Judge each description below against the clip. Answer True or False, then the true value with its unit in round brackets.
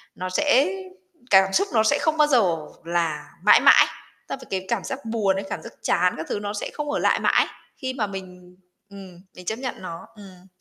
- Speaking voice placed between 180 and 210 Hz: True (195 Hz)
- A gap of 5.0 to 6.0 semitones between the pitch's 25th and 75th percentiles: True (5.4 semitones)